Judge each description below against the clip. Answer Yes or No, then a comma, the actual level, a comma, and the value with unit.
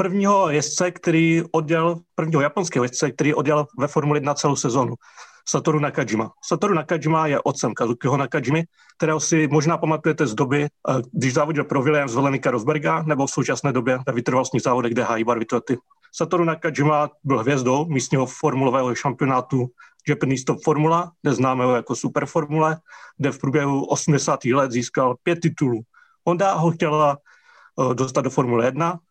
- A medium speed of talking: Yes, average, 155 wpm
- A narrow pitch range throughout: No, average, 3.3 semitones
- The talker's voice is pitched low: No, medium, 150 Hz